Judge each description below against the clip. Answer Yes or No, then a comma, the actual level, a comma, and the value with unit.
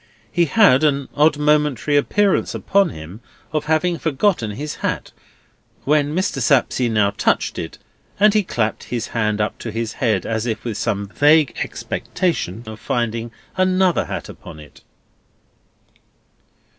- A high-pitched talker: No, low, 135 Hz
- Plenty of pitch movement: Yes, wide, 6.4 semitones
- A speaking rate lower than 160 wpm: Yes, average, 145 wpm